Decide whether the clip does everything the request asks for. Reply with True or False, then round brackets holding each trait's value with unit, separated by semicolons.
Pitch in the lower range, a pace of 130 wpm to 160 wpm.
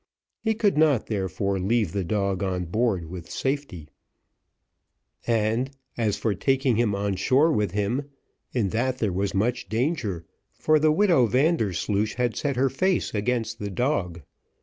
True (110 Hz; 150 wpm)